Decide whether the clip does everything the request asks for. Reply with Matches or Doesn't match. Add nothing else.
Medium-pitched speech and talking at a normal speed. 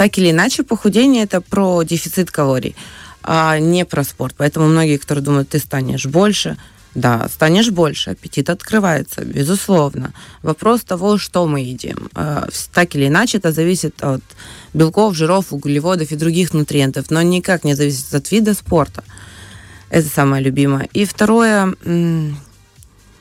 Matches